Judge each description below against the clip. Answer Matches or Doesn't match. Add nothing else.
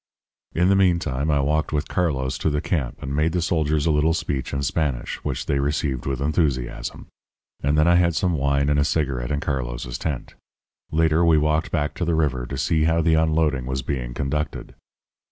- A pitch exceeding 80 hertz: Doesn't match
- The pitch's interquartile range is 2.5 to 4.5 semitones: Matches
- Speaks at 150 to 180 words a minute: Doesn't match